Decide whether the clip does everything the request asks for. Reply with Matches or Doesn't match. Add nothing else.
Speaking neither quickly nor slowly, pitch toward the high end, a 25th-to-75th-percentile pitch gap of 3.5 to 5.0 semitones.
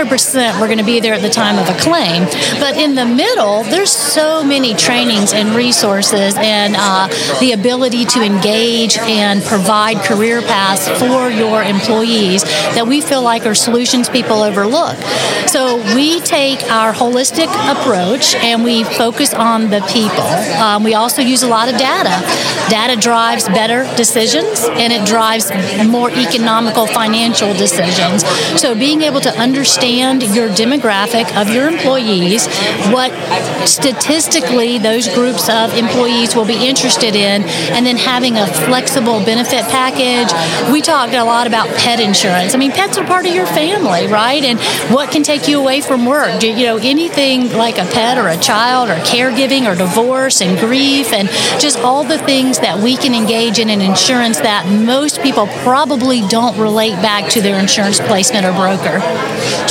Doesn't match